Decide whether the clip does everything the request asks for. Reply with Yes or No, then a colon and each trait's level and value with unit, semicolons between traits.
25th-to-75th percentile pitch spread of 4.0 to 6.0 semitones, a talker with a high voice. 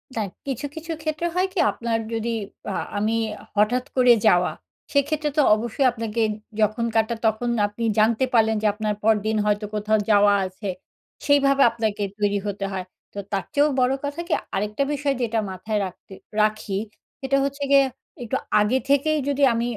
Yes: average, 4.6 semitones; high, 225 Hz